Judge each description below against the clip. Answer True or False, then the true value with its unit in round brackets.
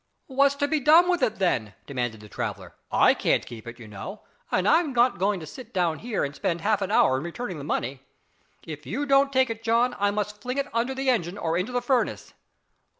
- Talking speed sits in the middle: False (230 wpm)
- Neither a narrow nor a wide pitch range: False (8.2 semitones)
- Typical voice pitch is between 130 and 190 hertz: False (210 Hz)